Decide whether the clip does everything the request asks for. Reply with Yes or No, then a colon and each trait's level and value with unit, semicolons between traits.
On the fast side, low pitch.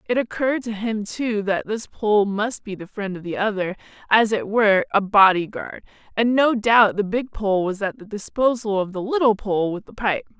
No: fast, 215 wpm; high, 210 Hz